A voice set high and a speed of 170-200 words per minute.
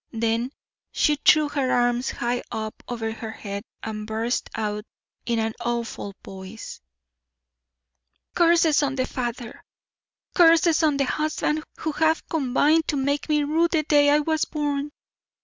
No: very high, 270 Hz; average, 145 wpm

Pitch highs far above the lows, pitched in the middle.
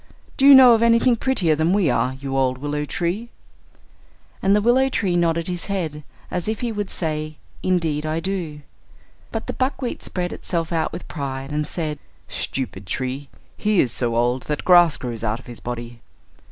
Yes: wide, 6.5 semitones; medium, 160 Hz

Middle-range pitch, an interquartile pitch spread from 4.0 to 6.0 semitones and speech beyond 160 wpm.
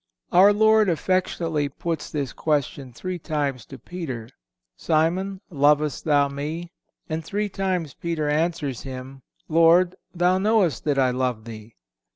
No: medium, 155 Hz; average, 4.4 semitones; slow, 135 wpm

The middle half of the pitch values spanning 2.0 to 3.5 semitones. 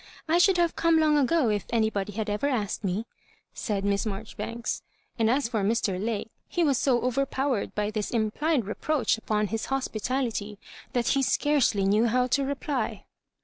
No: average, 4.6 semitones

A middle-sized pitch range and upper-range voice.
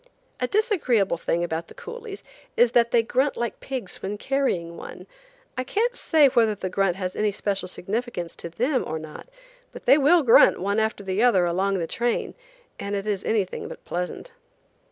No: wide, 5.8 semitones; high, 215 Hz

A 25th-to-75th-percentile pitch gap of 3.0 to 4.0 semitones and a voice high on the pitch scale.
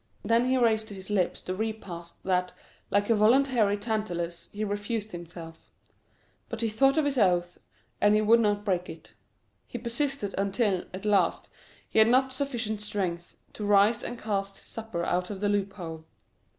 Yes: average, 3.5 semitones; high, 205 Hz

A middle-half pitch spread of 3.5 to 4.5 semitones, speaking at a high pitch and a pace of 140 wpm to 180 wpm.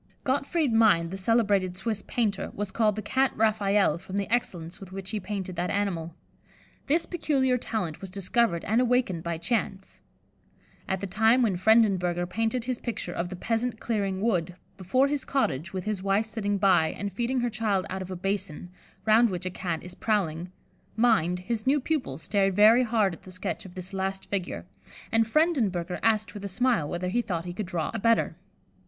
No: average, 3.9 semitones; high, 200 Hz; average, 195 wpm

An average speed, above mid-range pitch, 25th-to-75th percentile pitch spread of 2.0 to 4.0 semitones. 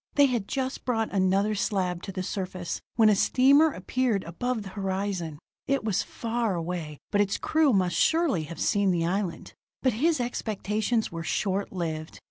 No: average, 170 wpm; high, 200 Hz; average, 4.9 semitones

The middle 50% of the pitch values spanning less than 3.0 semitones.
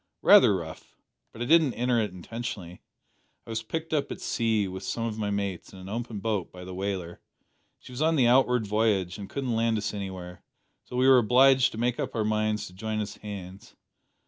No: average, 3.8 semitones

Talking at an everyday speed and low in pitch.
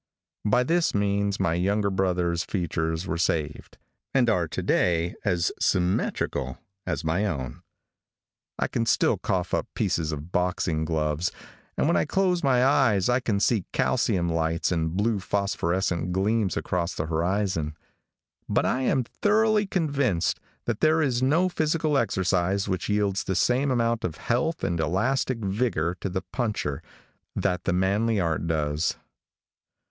Yes: average, 150 wpm; very low, 95 Hz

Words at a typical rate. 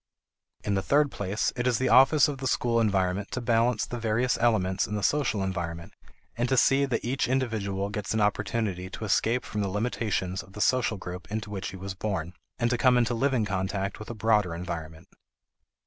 No: fast, 210 wpm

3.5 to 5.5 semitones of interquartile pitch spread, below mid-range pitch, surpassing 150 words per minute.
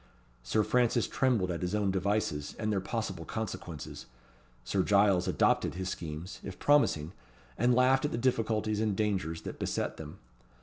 Yes: average, 4.0 semitones; low, 100 Hz; average, 160 wpm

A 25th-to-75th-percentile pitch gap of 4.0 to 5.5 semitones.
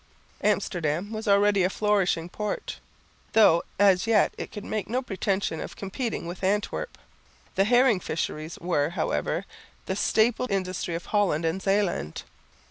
No: average, 3.3 semitones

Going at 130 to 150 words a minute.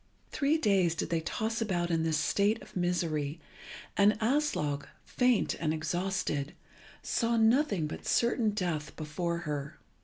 Yes: average, 140 wpm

